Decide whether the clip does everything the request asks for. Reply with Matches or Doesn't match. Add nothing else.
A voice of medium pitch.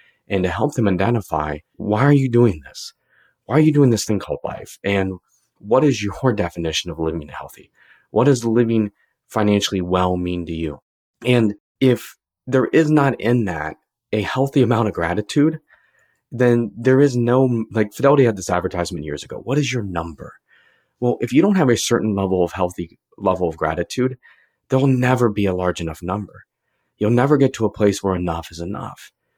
Doesn't match